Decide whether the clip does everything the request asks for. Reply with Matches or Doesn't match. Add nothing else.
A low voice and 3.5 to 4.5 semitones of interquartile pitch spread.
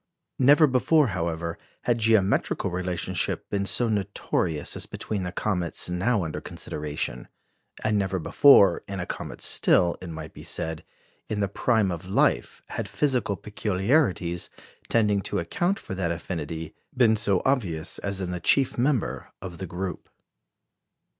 Matches